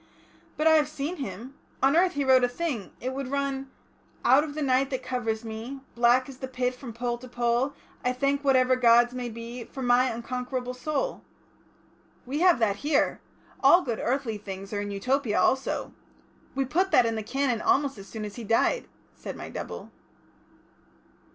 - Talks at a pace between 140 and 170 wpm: No, average, 185 wpm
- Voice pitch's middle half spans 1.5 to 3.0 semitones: Yes, average, 2.7 semitones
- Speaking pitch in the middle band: No, very high, 255 Hz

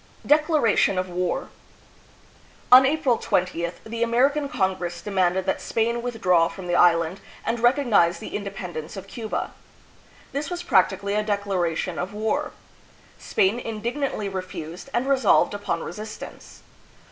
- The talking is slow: Yes, slow, 130 wpm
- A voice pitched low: No, high, 205 Hz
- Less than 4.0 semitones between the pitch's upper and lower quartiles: No, average, 4.9 semitones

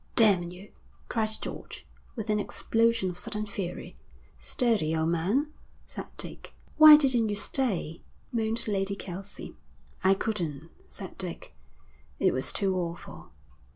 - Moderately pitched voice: No, high, 200 Hz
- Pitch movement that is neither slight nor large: Yes, average, 4.2 semitones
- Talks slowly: Yes, slow, 130 wpm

